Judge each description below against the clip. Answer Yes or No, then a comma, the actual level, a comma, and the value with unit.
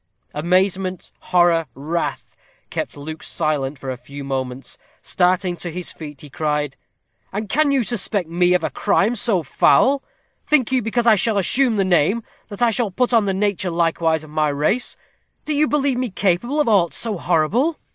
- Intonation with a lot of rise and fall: Yes, wide, 6.6 semitones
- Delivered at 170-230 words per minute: Yes, average, 180 wpm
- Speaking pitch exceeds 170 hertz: Yes, medium, 185 Hz